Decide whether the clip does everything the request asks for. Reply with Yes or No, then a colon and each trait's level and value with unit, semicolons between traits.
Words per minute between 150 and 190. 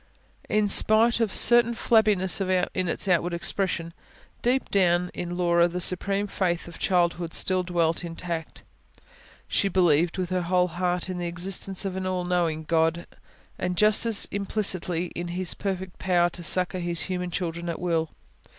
Yes: average, 165 wpm